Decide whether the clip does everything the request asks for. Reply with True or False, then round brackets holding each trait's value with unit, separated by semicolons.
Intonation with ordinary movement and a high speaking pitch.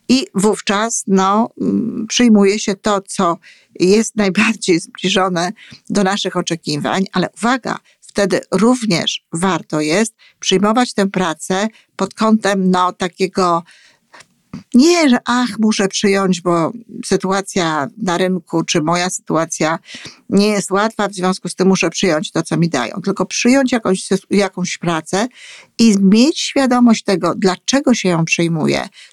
True (3.5 semitones; 195 Hz)